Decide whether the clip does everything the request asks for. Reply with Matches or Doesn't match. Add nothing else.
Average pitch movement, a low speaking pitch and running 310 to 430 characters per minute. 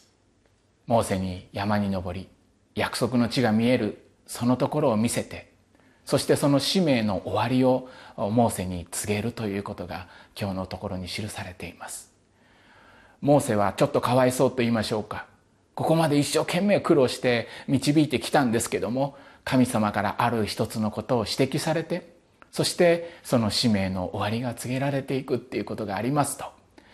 Matches